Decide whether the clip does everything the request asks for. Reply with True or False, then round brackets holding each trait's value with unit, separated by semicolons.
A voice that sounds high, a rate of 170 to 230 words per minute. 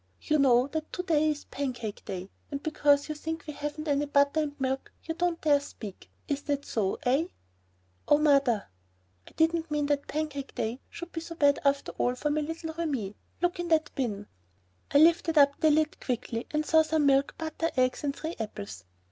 True (290 Hz; 200 wpm)